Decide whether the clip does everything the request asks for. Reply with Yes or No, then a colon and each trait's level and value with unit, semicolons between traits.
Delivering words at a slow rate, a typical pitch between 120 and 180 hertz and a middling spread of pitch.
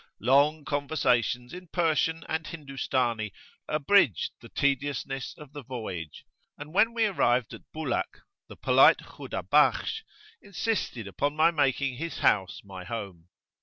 Yes: slow, 130 wpm; medium, 140 Hz; average, 4.9 semitones